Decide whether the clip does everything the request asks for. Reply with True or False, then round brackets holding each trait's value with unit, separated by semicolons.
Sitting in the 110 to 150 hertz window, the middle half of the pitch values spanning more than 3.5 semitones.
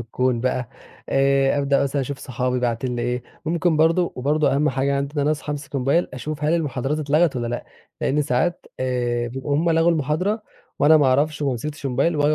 False (140 Hz; 3.1 semitones)